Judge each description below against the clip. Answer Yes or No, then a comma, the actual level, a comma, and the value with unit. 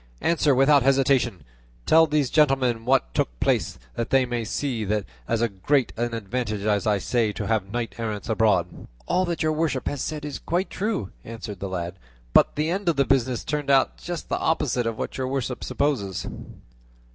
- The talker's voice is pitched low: Yes, low, 125 Hz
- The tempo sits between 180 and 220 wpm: Yes, average, 195 wpm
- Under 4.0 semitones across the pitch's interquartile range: No, average, 5.1 semitones